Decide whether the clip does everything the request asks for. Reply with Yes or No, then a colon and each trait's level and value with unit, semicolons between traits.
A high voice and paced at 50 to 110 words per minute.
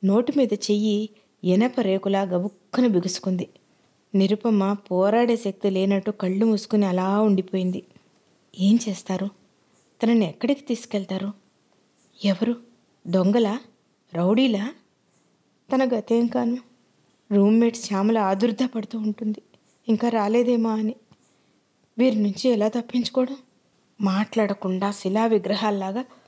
Yes: high, 215 Hz; average, 90 wpm